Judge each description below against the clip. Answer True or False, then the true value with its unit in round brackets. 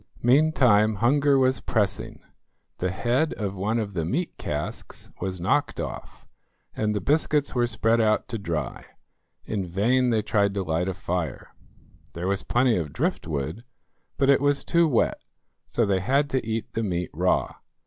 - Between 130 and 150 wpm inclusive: False (165 wpm)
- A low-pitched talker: True (110 Hz)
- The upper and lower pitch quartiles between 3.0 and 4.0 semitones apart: False (5.5 semitones)